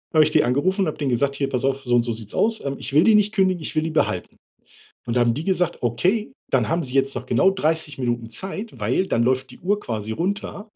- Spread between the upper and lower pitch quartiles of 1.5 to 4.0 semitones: No, wide, 7.2 semitones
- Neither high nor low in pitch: Yes, medium, 145 Hz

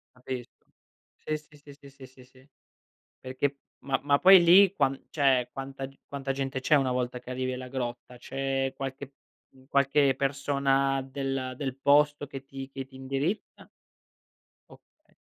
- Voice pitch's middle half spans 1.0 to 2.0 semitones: Yes, narrow, 1.3 semitones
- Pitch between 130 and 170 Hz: Yes, low, 135 Hz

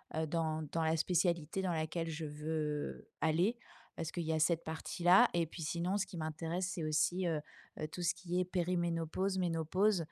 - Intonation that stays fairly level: Yes, narrow, 2.2 semitones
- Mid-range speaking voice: Yes, medium, 165 Hz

